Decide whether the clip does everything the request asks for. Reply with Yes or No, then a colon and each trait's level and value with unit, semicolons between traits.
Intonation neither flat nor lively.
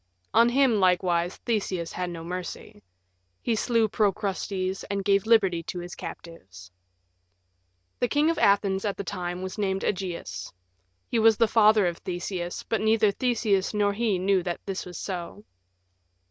Yes: average, 3.4 semitones